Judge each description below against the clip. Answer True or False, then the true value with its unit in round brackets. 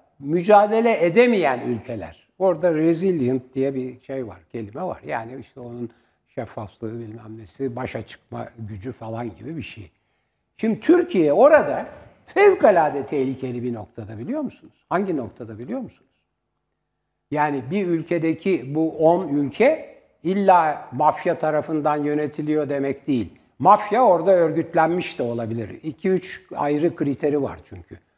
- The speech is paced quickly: False (125 wpm)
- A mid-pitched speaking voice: True (145 Hz)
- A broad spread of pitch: True (5.8 semitones)